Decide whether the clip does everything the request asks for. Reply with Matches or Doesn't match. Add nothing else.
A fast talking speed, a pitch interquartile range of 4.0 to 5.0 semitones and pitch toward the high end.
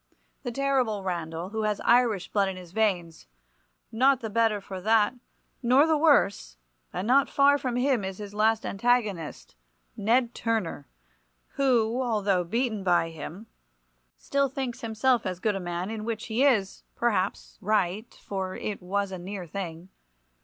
Doesn't match